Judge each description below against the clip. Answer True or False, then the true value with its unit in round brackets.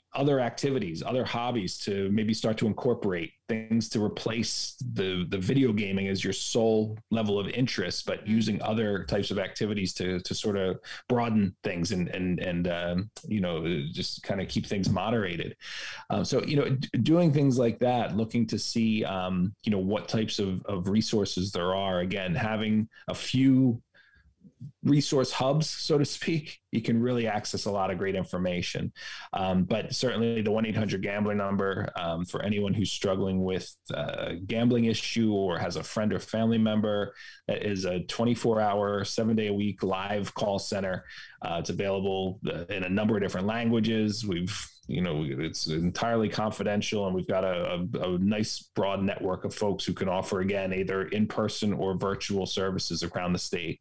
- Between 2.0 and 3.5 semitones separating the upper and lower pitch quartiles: True (3.0 semitones)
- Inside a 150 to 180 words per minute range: True (175 wpm)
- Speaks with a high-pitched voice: False (105 Hz)